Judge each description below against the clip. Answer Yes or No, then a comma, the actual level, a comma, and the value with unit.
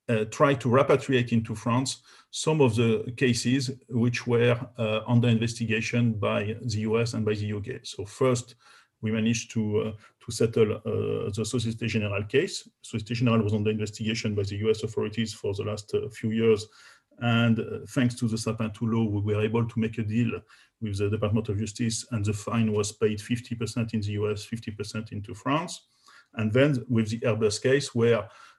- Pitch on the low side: Yes, low, 115 Hz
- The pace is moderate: Yes, average, 185 wpm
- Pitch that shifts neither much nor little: No, narrow, 1.8 semitones